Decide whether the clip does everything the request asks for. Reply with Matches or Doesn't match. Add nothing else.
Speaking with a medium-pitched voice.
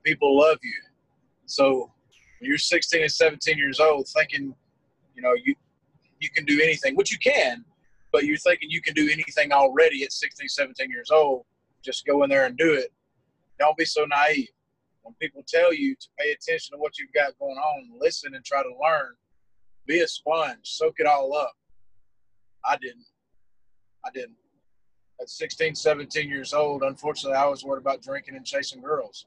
Matches